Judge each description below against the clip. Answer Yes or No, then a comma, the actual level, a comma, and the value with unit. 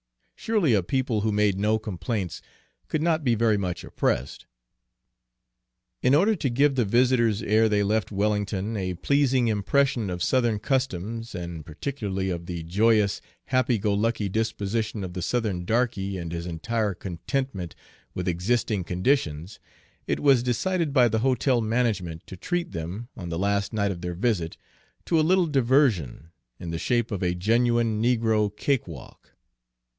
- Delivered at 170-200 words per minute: No, average, 155 wpm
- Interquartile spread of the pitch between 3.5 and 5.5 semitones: Yes, average, 5.1 semitones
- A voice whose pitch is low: Yes, low, 110 Hz